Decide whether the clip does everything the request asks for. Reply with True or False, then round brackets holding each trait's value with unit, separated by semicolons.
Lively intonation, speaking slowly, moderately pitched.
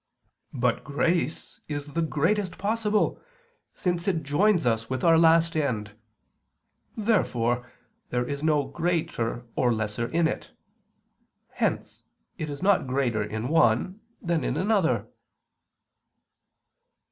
True (5.9 semitones; 115 wpm; 150 Hz)